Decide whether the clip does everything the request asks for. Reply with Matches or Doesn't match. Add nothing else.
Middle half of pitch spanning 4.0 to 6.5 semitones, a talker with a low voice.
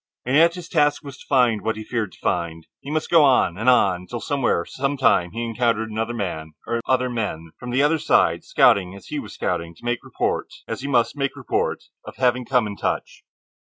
Matches